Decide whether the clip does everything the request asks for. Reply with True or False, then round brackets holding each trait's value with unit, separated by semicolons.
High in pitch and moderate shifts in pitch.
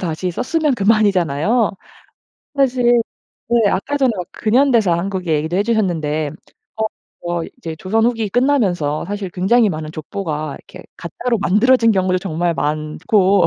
False (195 Hz; 5.7 semitones)